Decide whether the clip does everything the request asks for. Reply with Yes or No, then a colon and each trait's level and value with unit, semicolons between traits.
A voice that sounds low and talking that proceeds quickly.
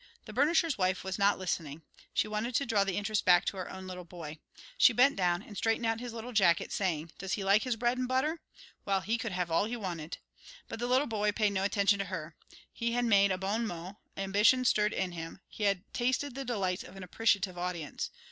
No: high, 200 Hz; fast, 230 wpm